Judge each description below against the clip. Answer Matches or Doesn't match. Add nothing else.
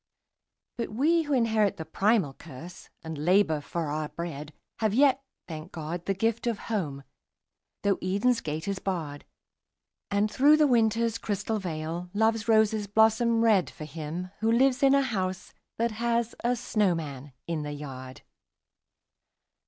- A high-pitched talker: Matches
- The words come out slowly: Doesn't match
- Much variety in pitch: Matches